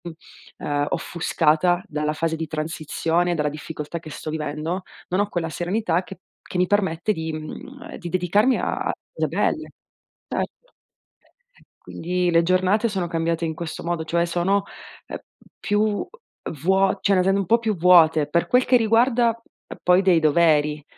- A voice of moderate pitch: Yes, medium, 175 Hz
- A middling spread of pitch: Yes, average, 3.6 semitones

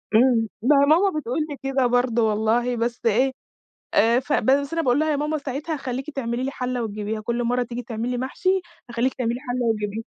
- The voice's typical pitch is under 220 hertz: No, high, 245 Hz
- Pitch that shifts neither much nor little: Yes, average, 3.0 semitones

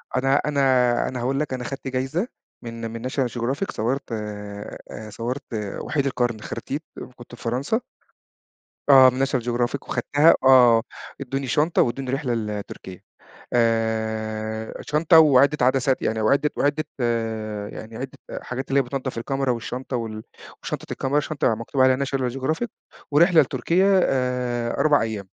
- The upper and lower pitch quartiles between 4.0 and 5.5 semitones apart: No, average, 3.2 semitones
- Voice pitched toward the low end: Yes, low, 130 Hz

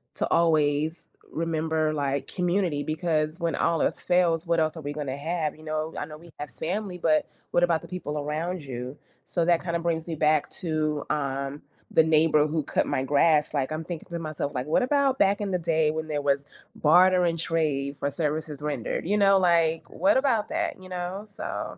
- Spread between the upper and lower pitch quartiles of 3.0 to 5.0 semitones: No, narrow, 2.6 semitones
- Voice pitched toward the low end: No, medium, 160 Hz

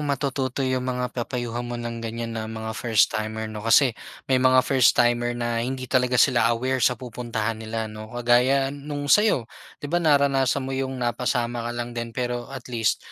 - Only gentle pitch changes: Yes, narrow, 2.2 semitones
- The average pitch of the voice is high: No, low, 120 Hz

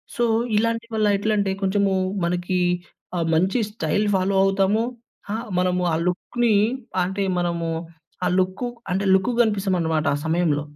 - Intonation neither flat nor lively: Yes, average, 3.0 semitones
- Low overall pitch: No, high, 190 Hz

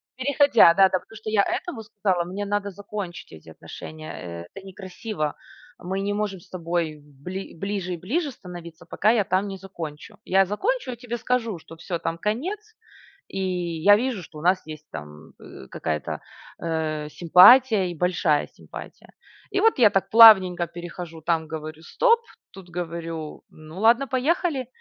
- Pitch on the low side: No, medium, 185 Hz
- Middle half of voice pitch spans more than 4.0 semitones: Yes, average, 4.9 semitones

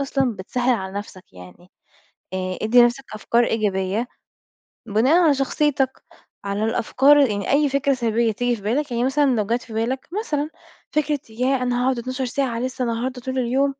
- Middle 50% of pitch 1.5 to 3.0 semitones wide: No, average, 3.5 semitones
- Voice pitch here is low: No, high, 245 Hz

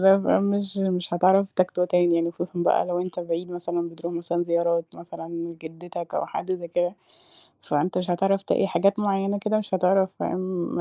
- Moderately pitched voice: Yes, medium, 180 Hz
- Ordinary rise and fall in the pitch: No, narrow, 2.1 semitones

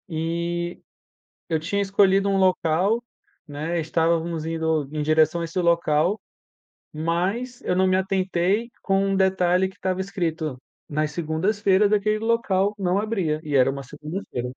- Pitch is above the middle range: No, medium, 175 Hz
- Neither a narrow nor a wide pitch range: Yes, average, 3.5 semitones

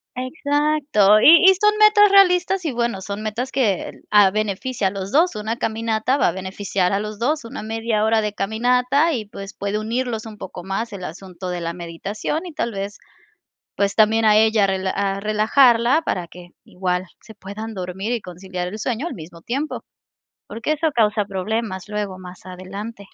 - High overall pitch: Yes, high, 215 Hz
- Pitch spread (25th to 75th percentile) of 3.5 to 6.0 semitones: Yes, average, 4.2 semitones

